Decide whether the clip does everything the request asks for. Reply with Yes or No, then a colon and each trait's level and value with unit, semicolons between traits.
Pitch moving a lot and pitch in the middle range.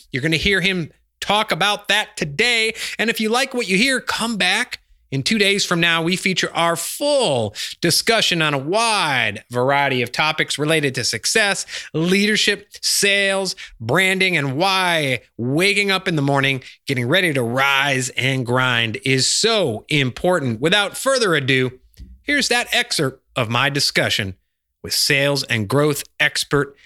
Yes: wide, 6.9 semitones; medium, 160 Hz